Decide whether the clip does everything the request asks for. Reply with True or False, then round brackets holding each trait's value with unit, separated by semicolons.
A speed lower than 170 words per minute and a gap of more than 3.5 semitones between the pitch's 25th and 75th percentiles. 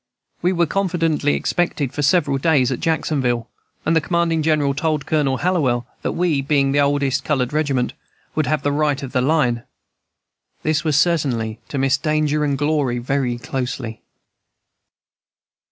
False (155 wpm; 2.9 semitones)